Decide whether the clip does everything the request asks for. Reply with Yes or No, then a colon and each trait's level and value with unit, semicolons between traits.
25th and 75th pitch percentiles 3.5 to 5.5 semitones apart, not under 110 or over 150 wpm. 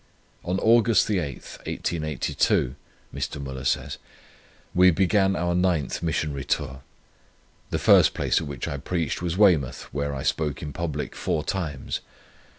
Yes: average, 4.3 semitones; average, 140 wpm